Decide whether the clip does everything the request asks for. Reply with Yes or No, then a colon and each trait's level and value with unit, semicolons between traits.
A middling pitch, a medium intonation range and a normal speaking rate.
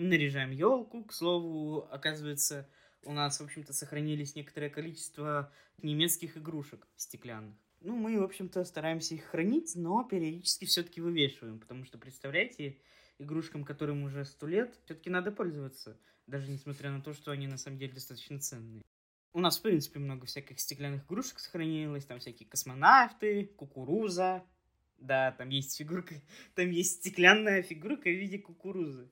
Yes: medium, 150 Hz; average, 4.4 semitones; average, 150 wpm